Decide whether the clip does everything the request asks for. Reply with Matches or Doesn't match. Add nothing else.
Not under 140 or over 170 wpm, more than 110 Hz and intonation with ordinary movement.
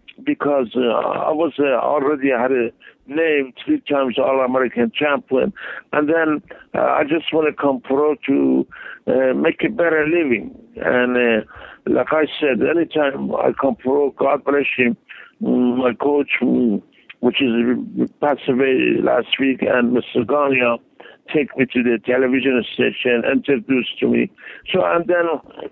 Matches